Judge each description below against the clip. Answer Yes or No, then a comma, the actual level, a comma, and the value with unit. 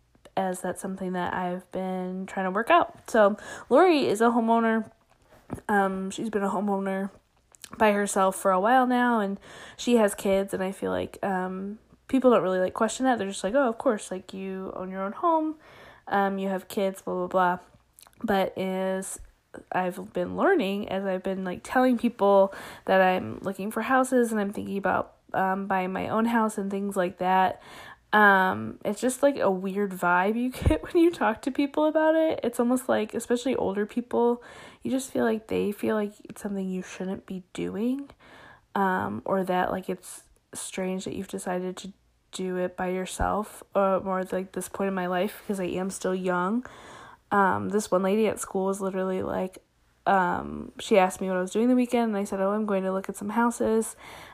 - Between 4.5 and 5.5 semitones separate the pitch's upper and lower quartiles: No, average, 3.2 semitones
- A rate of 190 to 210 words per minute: Yes, average, 200 wpm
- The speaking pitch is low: No, high, 195 Hz